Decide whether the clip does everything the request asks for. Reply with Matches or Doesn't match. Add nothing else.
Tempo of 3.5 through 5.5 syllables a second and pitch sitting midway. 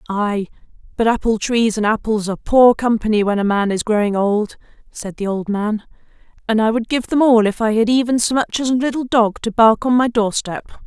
Doesn't match